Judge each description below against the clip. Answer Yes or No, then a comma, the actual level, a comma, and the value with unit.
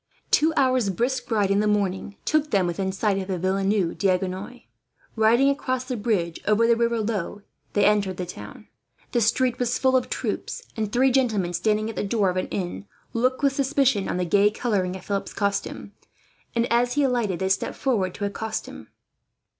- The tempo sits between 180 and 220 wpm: Yes, average, 190 wpm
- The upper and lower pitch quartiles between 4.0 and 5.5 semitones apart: Yes, average, 4.3 semitones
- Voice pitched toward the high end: Yes, high, 210 Hz